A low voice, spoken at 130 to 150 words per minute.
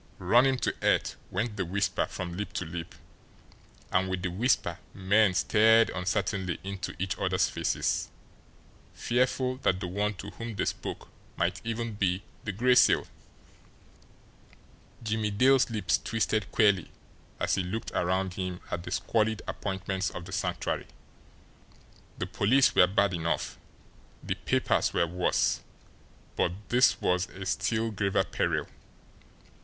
Yes: low, 100 Hz; average, 140 wpm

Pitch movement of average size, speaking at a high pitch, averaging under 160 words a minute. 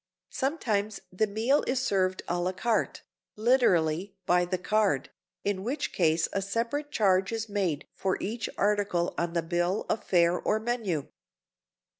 Yes: average, 3.9 semitones; high, 200 Hz; average, 150 wpm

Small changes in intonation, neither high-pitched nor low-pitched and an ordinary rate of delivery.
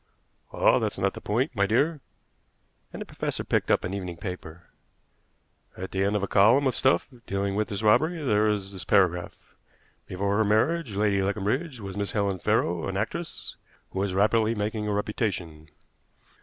No: narrow, 2.3 semitones; low, 100 Hz; average, 175 wpm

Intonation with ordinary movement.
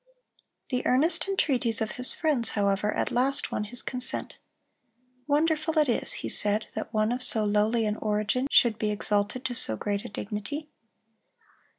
Yes: average, 3.8 semitones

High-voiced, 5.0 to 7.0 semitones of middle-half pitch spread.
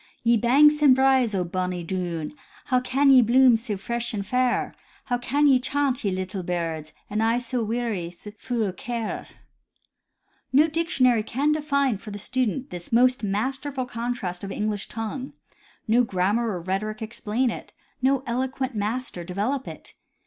No: high, 235 Hz; average, 4.3 semitones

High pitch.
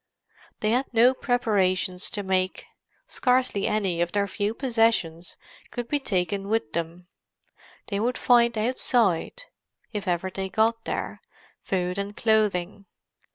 Yes: high, 205 Hz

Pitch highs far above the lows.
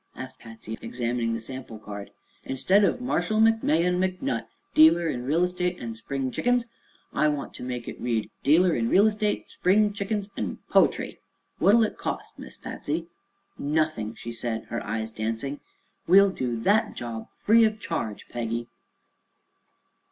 Yes: wide, 8.8 semitones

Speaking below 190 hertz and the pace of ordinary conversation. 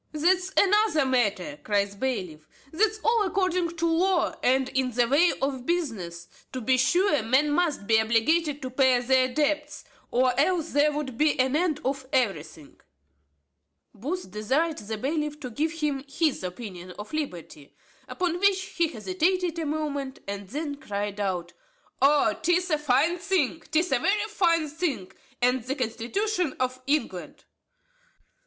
No: very high, 285 Hz; average, 155 wpm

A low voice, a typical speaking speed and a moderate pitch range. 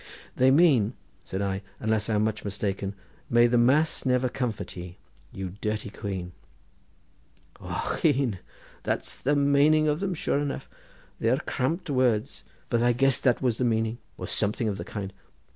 Yes: low, 120 Hz; average, 160 wpm; average, 4.5 semitones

